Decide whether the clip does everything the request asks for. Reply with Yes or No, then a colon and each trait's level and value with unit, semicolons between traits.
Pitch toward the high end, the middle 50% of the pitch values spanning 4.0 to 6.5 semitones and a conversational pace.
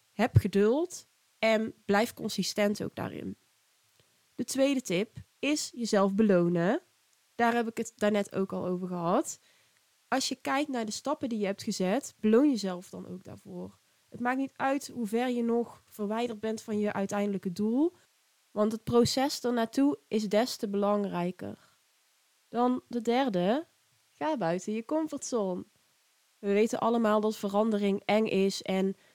No: high, 220 Hz; average, 3.5 semitones; average, 155 wpm